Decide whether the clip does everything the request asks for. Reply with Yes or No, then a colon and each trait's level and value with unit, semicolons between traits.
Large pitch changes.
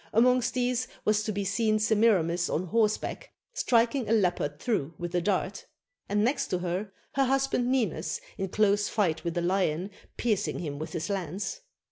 No: average, 4.7 semitones